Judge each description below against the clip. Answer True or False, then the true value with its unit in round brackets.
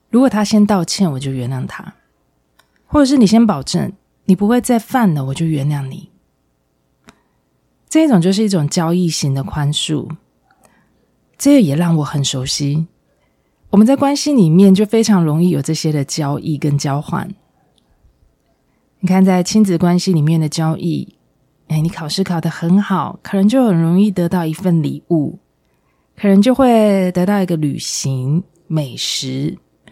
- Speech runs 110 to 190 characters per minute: False (230 characters per minute)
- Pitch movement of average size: True (4.7 semitones)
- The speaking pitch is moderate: True (175 Hz)